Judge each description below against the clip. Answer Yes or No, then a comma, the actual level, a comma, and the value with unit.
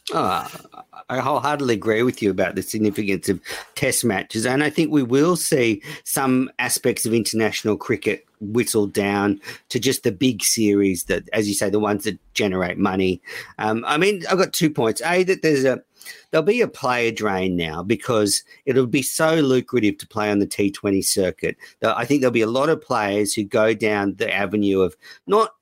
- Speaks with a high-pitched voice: No, low, 110 Hz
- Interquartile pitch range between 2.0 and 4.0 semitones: No, average, 4.7 semitones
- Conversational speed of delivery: Yes, average, 195 wpm